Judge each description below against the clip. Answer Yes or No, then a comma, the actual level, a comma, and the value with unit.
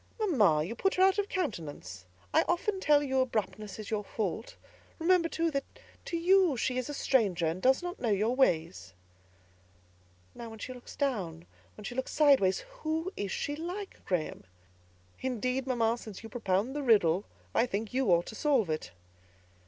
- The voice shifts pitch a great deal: Yes, wide, 7.1 semitones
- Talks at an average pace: Yes, average, 180 wpm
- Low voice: No, high, 245 Hz